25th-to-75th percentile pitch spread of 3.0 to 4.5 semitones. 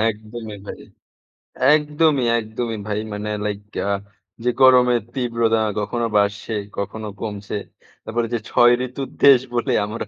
No: narrow, 2.6 semitones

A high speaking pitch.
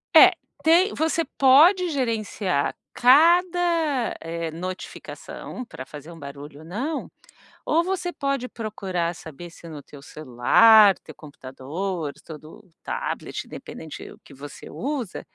Yes: high, 200 Hz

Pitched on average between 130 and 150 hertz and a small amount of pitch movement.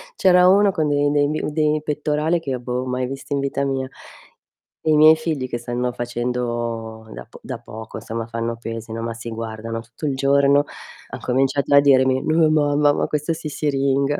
No: low, 135 Hz; average, 4.0 semitones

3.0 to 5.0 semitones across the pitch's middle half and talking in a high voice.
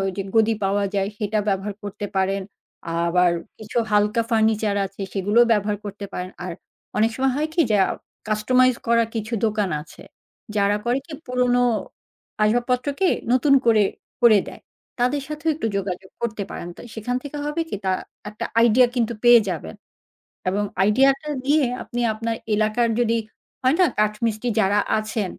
Yes: average, 3.3 semitones; high, 220 Hz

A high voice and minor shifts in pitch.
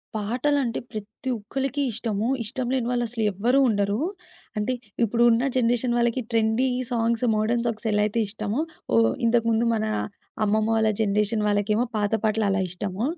Yes: high, 225 Hz; narrow, 2.2 semitones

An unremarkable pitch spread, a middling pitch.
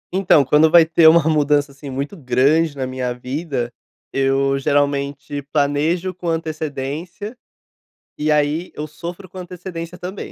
Yes: average, 3.3 semitones; medium, 150 Hz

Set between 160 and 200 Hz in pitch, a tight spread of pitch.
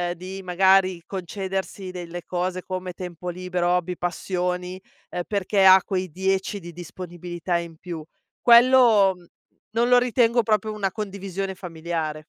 Yes: medium, 185 Hz; narrow, 1.8 semitones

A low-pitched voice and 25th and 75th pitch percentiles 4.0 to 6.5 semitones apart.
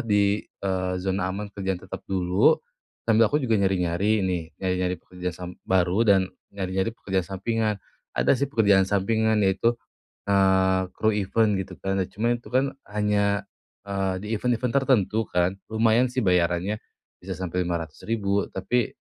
No: very low, 95 Hz; average, 2.7 semitones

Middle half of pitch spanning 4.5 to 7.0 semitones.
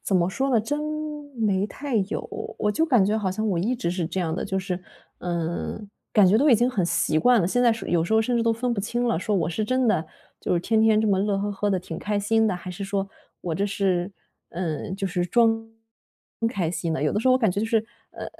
No: average, 3.7 semitones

